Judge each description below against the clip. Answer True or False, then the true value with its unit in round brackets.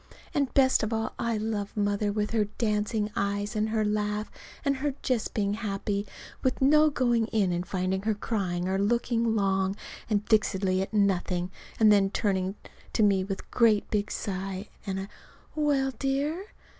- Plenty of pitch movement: False (2.8 semitones)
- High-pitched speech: True (210 Hz)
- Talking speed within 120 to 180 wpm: True (170 wpm)